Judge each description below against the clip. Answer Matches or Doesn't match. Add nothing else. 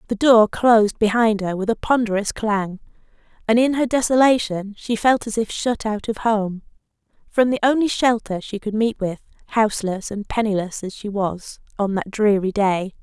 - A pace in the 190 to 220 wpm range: Doesn't match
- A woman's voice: Matches